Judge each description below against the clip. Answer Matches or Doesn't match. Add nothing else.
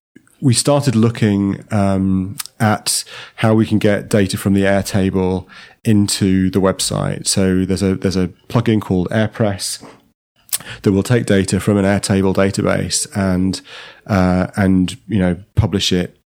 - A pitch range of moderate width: Doesn't match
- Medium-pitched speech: Doesn't match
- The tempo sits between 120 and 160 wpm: Matches